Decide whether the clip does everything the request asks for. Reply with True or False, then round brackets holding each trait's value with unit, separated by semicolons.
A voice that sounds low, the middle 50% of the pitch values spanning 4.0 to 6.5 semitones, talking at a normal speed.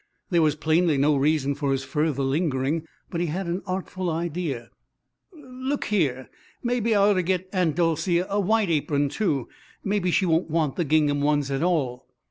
False (165 Hz; 4.3 semitones; 180 wpm)